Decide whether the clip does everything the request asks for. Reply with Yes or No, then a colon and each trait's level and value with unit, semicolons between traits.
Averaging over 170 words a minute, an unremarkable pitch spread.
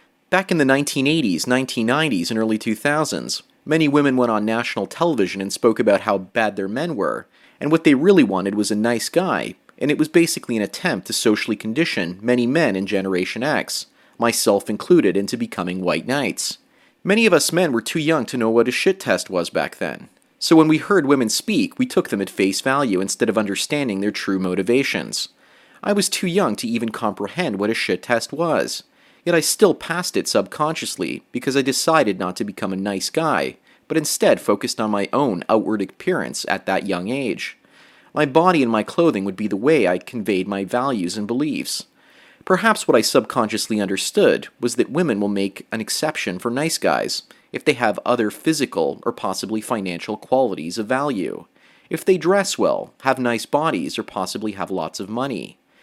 No: average, 190 wpm; wide, 7.7 semitones